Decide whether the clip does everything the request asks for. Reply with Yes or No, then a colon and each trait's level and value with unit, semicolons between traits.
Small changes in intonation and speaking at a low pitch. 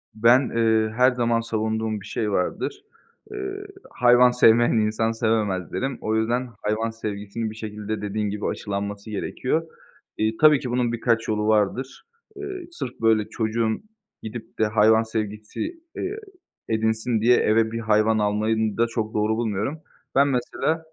Yes: narrow, 2.2 semitones; low, 110 Hz